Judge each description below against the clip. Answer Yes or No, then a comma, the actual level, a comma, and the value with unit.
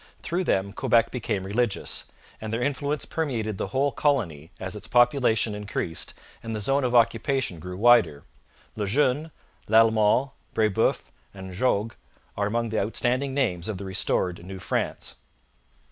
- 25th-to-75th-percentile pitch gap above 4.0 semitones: Yes, average, 4.5 semitones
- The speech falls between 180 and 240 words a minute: No, average, 145 wpm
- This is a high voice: No, low, 110 Hz